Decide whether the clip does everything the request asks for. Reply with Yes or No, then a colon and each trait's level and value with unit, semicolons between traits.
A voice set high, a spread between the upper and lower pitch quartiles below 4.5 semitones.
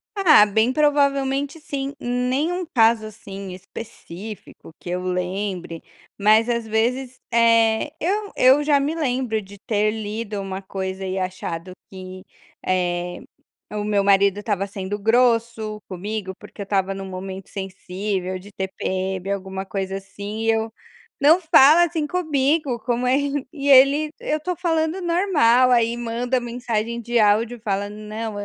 No: high, 220 Hz; average, 5.3 semitones